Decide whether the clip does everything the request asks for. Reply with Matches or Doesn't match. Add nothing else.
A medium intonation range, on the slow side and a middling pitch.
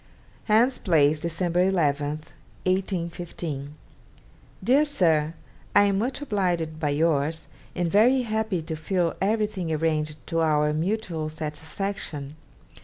Matches